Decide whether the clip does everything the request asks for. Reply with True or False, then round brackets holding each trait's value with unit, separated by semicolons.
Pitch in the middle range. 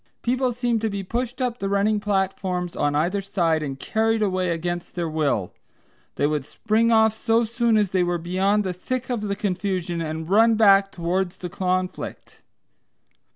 False (195 Hz)